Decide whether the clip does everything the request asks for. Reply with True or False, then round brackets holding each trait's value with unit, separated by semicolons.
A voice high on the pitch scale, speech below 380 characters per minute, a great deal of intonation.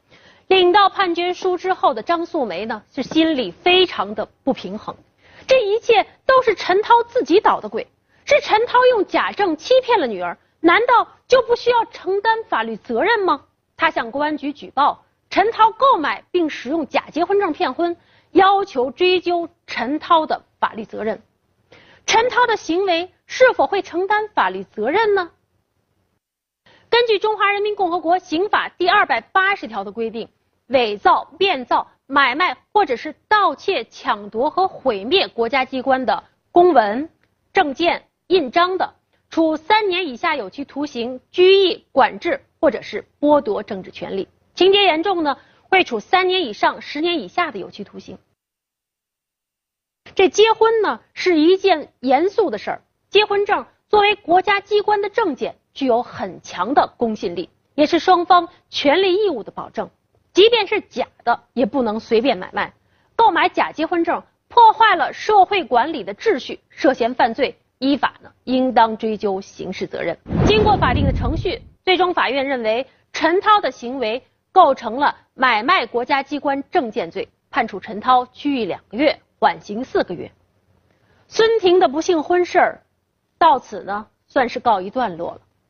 True (355 Hz; 240 characters per minute; 6.8 semitones)